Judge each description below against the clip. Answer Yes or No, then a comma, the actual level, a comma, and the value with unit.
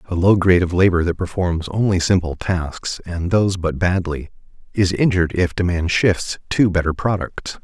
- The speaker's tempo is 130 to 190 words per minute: Yes, average, 175 wpm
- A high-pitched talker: No, very low, 90 Hz